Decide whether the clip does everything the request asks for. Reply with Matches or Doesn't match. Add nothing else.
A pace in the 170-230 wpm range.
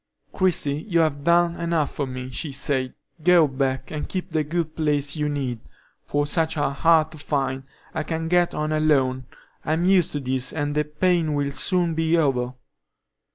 Matches